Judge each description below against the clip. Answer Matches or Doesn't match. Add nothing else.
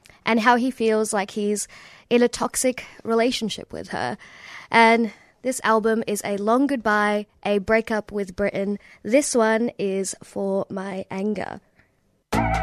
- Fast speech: Doesn't match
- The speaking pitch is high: Matches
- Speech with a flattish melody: Matches